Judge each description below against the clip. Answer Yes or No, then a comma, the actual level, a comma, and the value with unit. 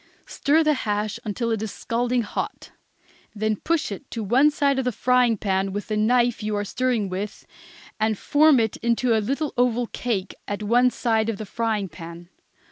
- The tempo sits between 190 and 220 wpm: Yes, average, 195 wpm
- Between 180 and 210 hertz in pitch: No, high, 225 Hz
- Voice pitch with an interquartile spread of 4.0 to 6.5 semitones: No, average, 3.2 semitones